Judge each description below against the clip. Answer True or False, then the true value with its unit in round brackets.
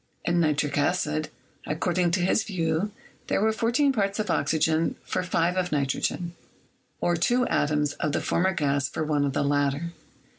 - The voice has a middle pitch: True (165 Hz)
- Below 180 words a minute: True (170 wpm)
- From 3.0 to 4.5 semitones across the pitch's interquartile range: True (3.8 semitones)